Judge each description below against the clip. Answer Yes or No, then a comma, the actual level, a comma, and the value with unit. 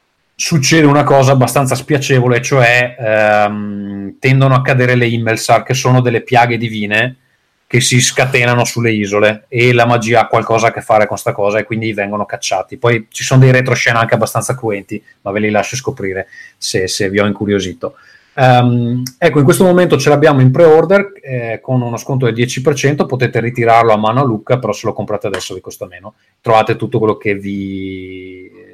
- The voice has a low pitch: Yes, low, 120 Hz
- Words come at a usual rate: No, fast, 185 wpm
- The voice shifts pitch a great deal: No, average, 3.4 semitones